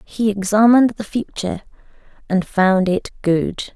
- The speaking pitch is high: Yes, high, 200 Hz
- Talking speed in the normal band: No, slow, 130 wpm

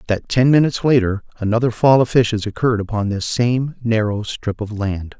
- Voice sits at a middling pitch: No, low, 115 Hz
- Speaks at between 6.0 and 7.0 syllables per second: No, 5.4 syllables/s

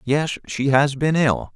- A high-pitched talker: No, medium, 140 Hz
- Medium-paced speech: Yes, average, 195 wpm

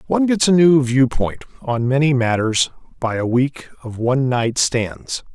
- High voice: No, low, 130 Hz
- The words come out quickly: No, average, 170 wpm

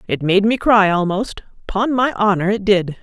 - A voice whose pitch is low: No, high, 200 Hz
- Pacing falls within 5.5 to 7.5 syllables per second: No, 4.7 syllables/s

